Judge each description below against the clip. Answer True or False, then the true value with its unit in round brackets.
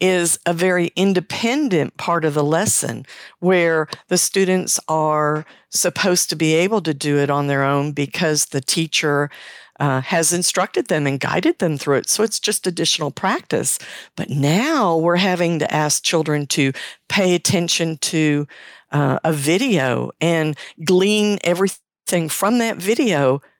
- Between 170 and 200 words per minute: False (150 wpm)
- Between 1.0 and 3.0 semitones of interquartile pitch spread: False (3.7 semitones)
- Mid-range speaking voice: True (165 Hz)